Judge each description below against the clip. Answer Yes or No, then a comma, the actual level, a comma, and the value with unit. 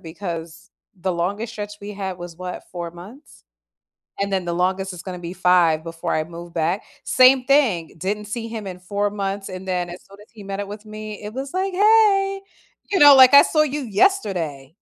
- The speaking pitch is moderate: No, high, 195 Hz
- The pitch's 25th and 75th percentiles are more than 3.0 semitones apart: Yes, average, 4.6 semitones